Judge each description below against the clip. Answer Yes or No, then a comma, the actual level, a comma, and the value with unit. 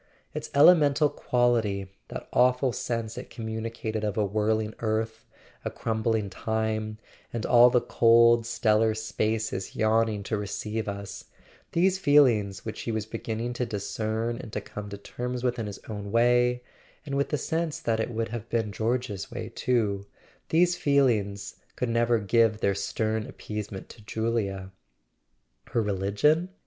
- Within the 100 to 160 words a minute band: Yes, average, 150 wpm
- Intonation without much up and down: Yes, narrow, 2.3 semitones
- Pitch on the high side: No, low, 110 Hz